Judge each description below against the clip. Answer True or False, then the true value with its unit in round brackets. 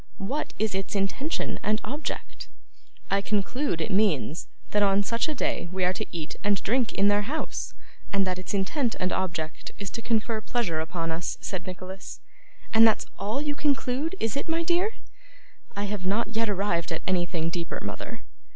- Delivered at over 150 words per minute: True (180 wpm)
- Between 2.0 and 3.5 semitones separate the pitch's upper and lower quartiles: False (4.2 semitones)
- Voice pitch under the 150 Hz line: False (205 Hz)